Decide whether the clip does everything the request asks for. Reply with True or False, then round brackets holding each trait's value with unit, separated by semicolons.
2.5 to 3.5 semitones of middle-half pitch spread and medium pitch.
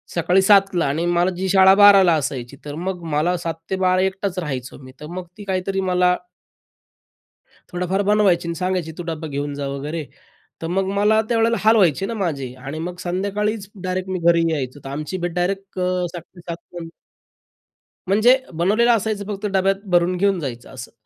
True (2.9 semitones; 180 Hz)